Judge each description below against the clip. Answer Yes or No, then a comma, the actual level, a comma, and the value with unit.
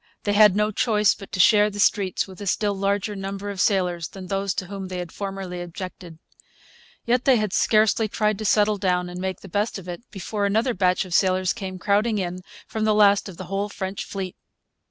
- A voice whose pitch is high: Yes, high, 195 Hz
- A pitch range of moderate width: No, narrow, 2.1 semitones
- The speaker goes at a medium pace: No, fast, 215 wpm